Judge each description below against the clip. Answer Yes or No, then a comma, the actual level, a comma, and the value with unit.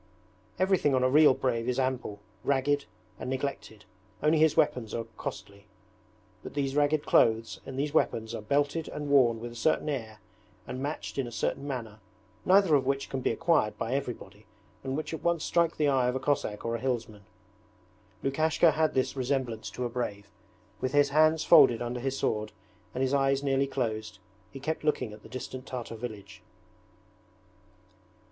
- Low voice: Yes, low, 130 Hz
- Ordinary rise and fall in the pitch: Yes, average, 3.8 semitones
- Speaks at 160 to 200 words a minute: Yes, average, 180 wpm